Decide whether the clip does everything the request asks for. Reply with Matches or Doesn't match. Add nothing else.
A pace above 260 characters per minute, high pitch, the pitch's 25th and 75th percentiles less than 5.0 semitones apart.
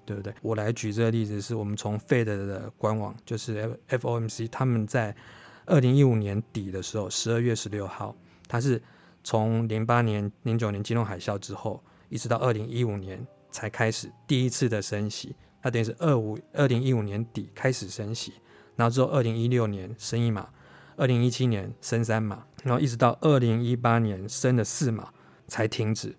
Doesn't match